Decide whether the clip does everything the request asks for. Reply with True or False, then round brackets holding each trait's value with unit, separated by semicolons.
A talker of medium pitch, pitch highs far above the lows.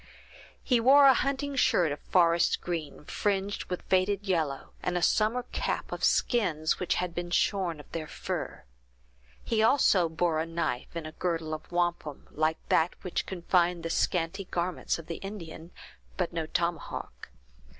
False (175 Hz; 3.1 semitones)